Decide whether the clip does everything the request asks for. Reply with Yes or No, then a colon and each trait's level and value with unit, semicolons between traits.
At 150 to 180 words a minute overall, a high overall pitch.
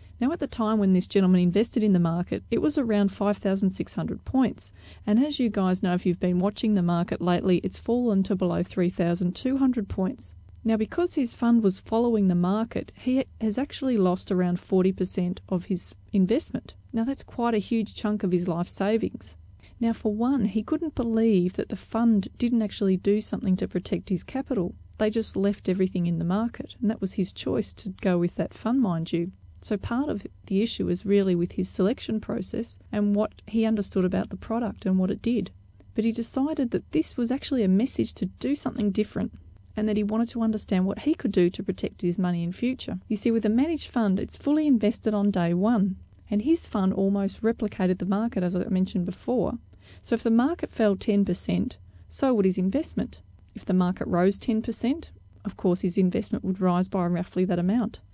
No: fast, 205 wpm; high, 205 Hz